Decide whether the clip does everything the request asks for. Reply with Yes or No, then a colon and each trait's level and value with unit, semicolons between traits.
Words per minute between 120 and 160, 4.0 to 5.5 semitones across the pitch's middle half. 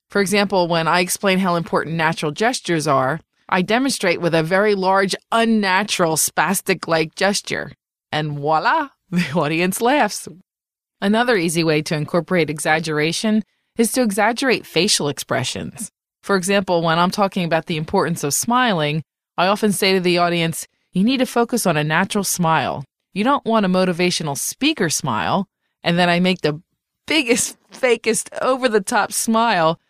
Yes: average, 155 wpm; average, 4.7 semitones